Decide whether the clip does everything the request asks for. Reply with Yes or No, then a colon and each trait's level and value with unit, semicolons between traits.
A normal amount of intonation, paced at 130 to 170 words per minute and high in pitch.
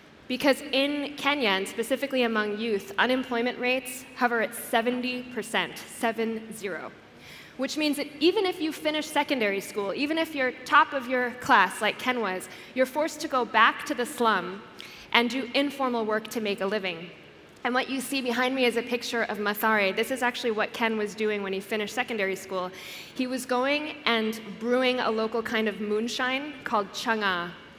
No: average, 3.6 semitones; average, 180 wpm; high, 240 Hz